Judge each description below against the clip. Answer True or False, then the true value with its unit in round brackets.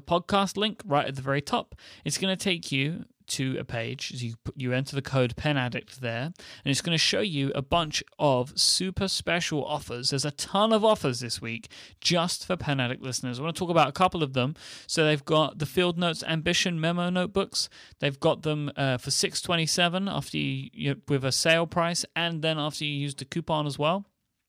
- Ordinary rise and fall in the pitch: True (4.2 semitones)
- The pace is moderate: False (210 wpm)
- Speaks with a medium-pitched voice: True (150 Hz)